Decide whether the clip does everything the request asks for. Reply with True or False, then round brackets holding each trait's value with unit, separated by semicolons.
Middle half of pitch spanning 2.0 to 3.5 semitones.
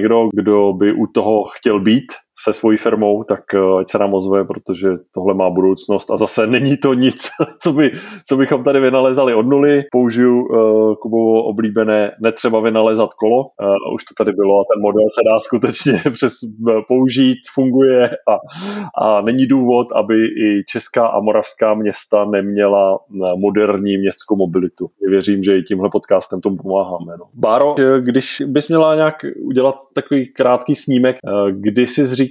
False (4.4 semitones)